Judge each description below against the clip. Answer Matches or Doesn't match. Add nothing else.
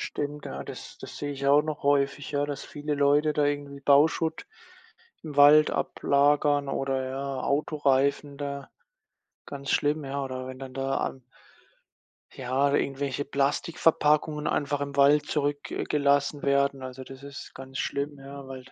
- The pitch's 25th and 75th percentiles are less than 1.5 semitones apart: Matches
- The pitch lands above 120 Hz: Matches